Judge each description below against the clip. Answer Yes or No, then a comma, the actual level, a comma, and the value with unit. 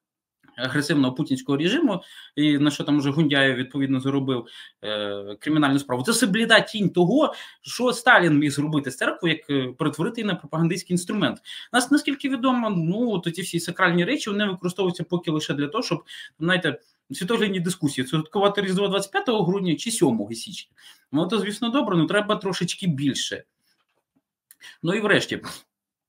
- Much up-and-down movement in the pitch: Yes, wide, 5.9 semitones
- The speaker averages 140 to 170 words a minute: Yes, average, 150 wpm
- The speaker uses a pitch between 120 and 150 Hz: No, medium, 170 Hz